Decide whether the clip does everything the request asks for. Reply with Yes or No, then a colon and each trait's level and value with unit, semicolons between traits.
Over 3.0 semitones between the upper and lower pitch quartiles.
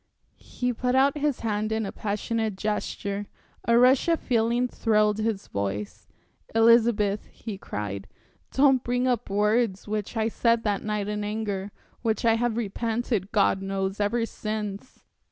No: narrow, 2.6 semitones